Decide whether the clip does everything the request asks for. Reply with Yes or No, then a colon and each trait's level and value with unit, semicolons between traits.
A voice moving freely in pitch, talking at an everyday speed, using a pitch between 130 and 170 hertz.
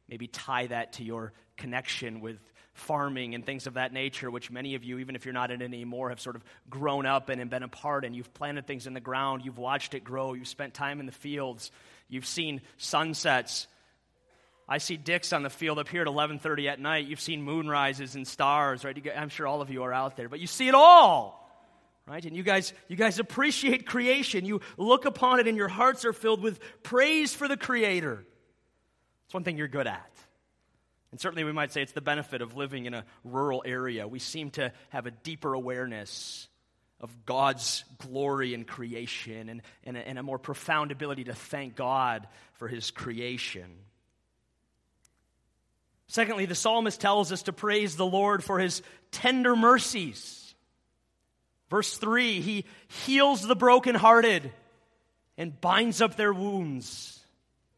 Yes: wide, 7.3 semitones; average, 185 wpm; medium, 140 Hz